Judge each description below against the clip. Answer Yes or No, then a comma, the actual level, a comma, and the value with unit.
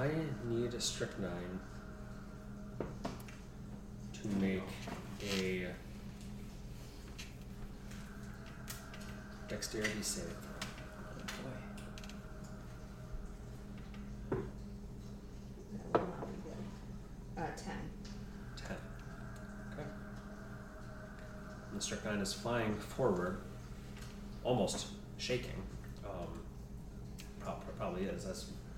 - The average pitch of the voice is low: Yes, very low, 65 Hz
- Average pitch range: No, wide, 7.3 semitones